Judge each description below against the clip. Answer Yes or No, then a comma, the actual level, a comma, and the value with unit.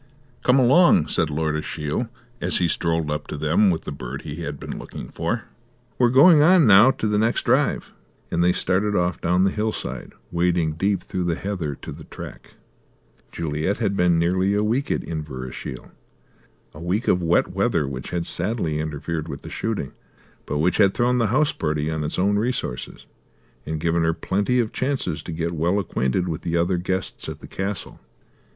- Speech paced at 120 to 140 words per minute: No, average, 190 wpm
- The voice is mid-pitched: No, very low, 85 Hz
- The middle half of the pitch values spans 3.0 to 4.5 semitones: No, average, 4.9 semitones